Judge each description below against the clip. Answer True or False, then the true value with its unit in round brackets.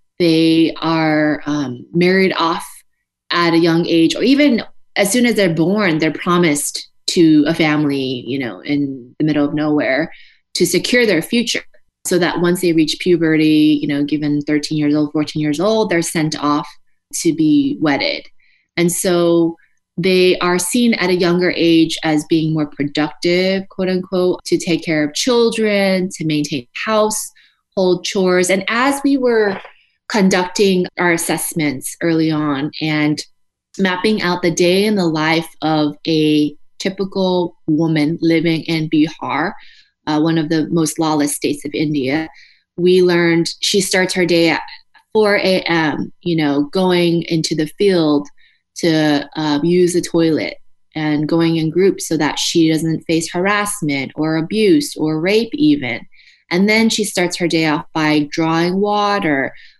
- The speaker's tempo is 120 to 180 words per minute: True (155 wpm)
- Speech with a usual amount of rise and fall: True (3.4 semitones)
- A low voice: False (165 Hz)